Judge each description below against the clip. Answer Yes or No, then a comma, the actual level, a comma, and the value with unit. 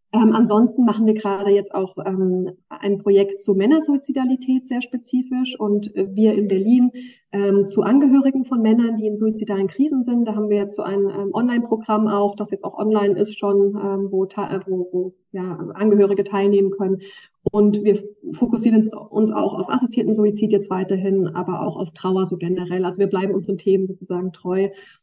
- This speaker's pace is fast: No, average, 180 wpm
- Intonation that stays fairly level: Yes, narrow, 2.3 semitones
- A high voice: Yes, high, 205 Hz